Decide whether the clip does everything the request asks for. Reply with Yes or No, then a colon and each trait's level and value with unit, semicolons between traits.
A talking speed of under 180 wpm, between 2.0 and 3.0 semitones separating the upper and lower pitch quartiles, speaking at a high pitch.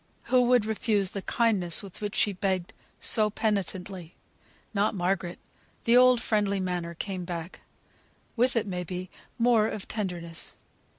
No: average, 140 wpm; average, 3.4 semitones; high, 200 Hz